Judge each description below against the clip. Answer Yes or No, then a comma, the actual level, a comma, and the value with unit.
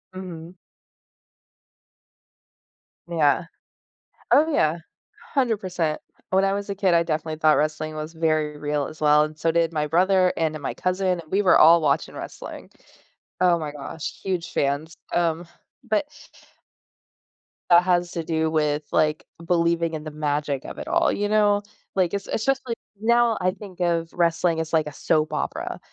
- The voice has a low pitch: No, medium, 165 Hz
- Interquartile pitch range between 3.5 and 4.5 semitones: No, average, 3.1 semitones